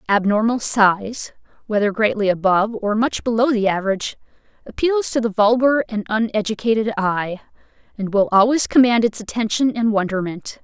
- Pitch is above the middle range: Yes, high, 220 Hz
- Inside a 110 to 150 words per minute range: Yes, average, 140 wpm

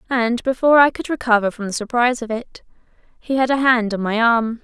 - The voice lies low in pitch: No, high, 235 Hz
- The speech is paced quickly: Yes, fast, 220 wpm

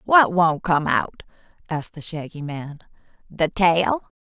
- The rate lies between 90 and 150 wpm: Yes, average, 140 wpm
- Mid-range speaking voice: Yes, medium, 165 Hz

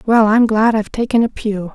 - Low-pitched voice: No, high, 220 Hz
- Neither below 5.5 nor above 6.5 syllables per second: Yes, 5.6 syllables/s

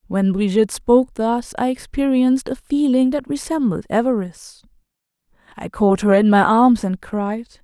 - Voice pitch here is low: No, high, 230 Hz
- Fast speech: No, average, 150 wpm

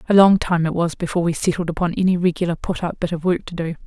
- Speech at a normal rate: No, fast, 280 wpm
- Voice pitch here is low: No, medium, 175 Hz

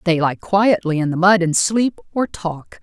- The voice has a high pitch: No, medium, 175 Hz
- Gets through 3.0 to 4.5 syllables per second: Yes, 4.2 syllables/s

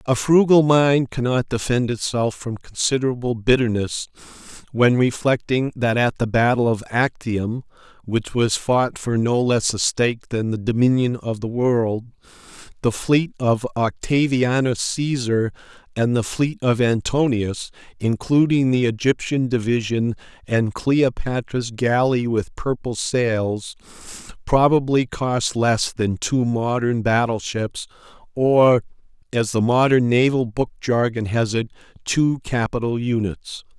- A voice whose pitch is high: No, low, 120 Hz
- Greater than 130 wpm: No, slow, 125 wpm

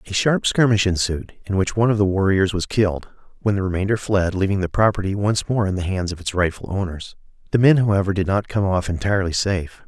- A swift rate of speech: Yes, fast, 225 wpm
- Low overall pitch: Yes, very low, 95 Hz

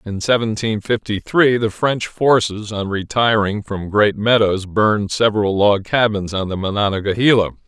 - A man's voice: Yes, male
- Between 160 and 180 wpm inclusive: No, average, 150 wpm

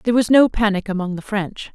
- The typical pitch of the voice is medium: No, high, 210 Hz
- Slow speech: No, fast, 240 wpm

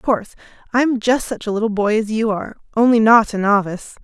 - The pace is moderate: No, fast, 240 wpm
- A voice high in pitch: Yes, high, 220 Hz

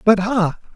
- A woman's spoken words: No, male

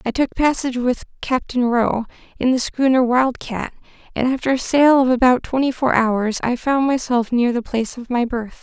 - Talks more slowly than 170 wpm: No, average, 200 wpm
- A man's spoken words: No, female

